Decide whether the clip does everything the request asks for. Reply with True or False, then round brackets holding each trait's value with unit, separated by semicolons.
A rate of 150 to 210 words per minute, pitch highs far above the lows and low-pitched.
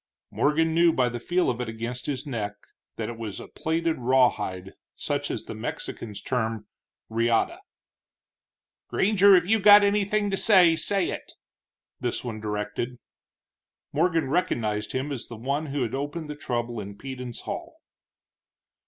True (155 wpm; 6.4 semitones; 130 Hz)